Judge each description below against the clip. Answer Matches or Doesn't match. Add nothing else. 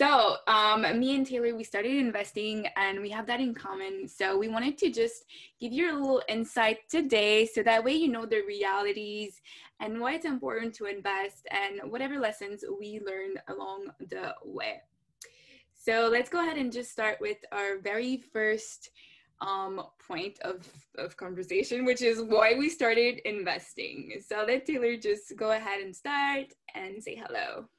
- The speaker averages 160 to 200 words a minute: Matches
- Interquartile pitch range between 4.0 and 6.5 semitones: Matches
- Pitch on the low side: Doesn't match